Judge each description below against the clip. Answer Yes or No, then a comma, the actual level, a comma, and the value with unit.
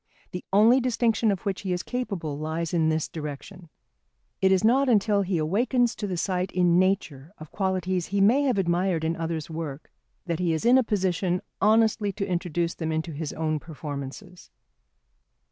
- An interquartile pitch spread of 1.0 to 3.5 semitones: No, average, 4.1 semitones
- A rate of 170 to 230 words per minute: Yes, average, 180 wpm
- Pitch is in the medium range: Yes, medium, 180 Hz